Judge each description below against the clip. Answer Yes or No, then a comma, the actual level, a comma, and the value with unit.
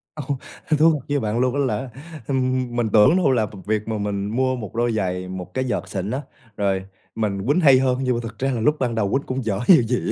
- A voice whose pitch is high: No, low, 120 Hz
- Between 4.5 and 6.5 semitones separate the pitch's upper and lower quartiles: No, average, 3.8 semitones